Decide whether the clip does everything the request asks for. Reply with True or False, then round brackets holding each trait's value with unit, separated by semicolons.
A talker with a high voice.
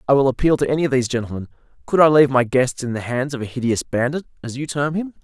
False (135 Hz)